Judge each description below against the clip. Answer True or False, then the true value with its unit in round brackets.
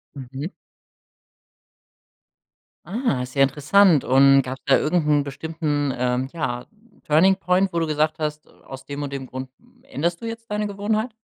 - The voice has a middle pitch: True (150 Hz)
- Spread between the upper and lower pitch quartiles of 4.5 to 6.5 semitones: True (5.5 semitones)